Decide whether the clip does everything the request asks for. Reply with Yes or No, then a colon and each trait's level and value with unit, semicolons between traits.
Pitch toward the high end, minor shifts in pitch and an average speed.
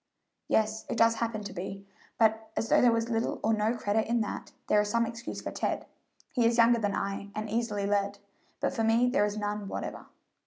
No: high, 220 Hz; narrow, 1.9 semitones; fast, 220 wpm